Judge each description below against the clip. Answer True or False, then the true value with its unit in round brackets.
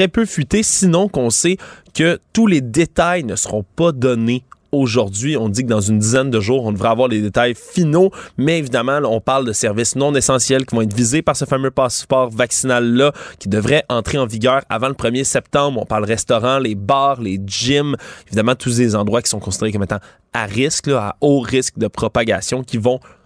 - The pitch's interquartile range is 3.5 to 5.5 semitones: True (4.0 semitones)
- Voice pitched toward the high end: False (130 Hz)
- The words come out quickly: False (210 wpm)